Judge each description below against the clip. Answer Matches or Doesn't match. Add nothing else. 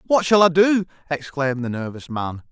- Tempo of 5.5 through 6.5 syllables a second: Doesn't match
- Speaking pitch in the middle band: Matches